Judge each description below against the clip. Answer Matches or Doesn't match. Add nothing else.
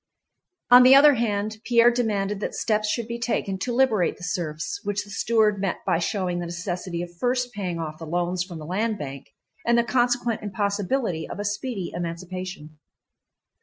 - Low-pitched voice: Doesn't match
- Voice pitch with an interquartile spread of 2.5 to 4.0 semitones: Doesn't match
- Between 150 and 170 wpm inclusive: Doesn't match